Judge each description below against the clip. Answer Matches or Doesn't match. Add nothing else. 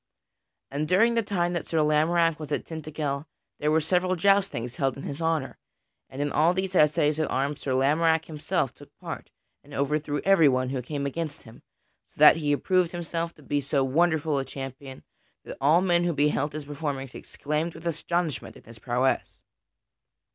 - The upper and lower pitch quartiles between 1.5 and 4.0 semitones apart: Matches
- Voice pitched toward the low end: Doesn't match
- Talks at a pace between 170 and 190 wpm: Matches